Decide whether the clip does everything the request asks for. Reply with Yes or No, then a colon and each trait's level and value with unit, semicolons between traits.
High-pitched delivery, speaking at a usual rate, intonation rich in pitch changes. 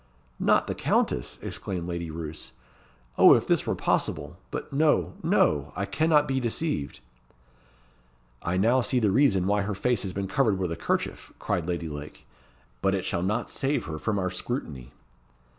No: very low, 95 Hz; average, 170 wpm; wide, 6.5 semitones